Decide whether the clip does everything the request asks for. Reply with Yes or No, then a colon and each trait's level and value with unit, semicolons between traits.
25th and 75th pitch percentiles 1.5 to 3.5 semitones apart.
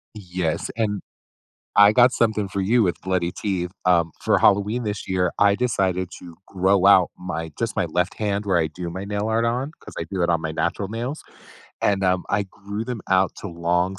Yes: average, 2.8 semitones